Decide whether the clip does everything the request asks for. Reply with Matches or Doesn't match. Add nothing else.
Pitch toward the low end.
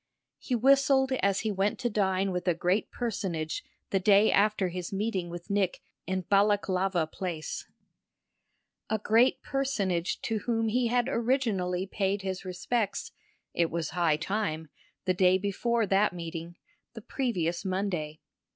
Doesn't match